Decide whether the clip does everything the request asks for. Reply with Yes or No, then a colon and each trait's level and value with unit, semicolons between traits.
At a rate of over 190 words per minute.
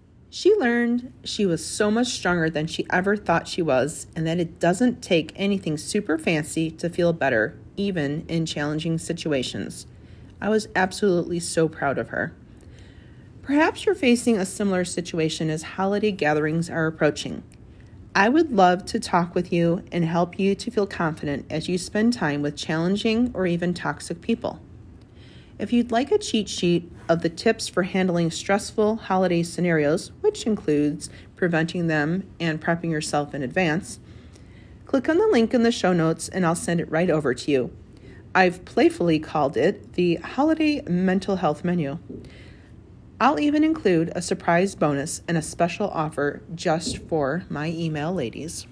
No: average, 165 wpm